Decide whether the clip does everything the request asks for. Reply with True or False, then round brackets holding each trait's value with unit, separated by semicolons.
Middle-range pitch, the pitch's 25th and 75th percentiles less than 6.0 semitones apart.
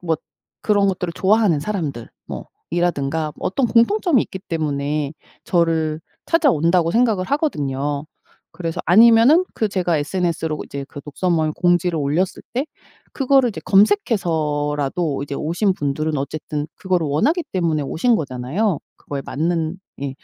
True (170 Hz; 5.4 semitones)